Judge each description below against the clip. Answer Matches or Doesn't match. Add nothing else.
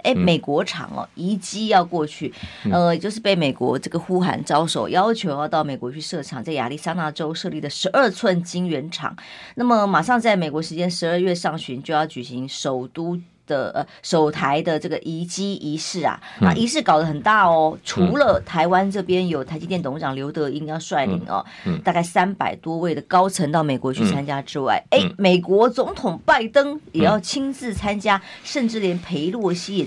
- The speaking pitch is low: Doesn't match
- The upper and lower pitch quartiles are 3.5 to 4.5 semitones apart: Matches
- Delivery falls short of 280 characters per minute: Doesn't match